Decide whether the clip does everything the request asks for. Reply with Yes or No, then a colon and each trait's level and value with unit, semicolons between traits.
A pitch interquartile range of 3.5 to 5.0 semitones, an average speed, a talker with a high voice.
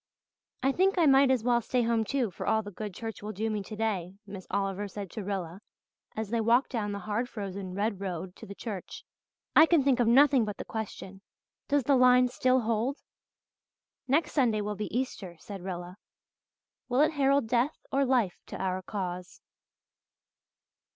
Yes: average, 4.4 semitones; average, 185 wpm; high, 220 Hz